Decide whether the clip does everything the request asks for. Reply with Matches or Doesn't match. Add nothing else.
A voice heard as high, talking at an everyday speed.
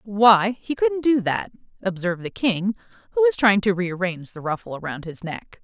Matches